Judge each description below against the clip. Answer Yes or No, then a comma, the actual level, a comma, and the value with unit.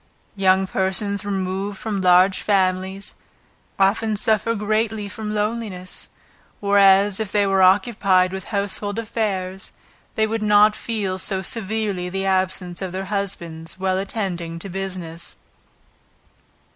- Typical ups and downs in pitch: No, narrow, 1.9 semitones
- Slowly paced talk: Yes, slow, 120 wpm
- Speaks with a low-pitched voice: No, high, 195 Hz